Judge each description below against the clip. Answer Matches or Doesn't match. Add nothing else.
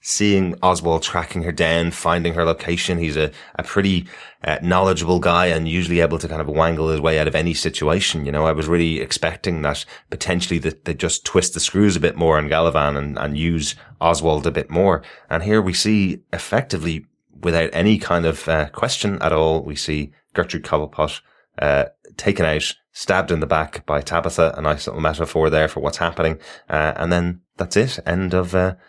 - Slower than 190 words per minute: Doesn't match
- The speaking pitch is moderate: Doesn't match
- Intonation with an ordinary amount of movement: Doesn't match